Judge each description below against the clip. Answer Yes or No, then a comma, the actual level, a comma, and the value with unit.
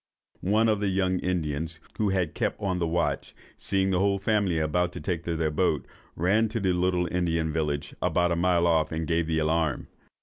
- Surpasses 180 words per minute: Yes, average, 200 wpm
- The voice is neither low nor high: No, very low, 90 Hz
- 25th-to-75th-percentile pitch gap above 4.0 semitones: No, average, 2.8 semitones